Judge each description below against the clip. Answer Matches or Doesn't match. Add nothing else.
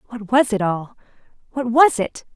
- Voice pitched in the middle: Doesn't match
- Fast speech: Doesn't match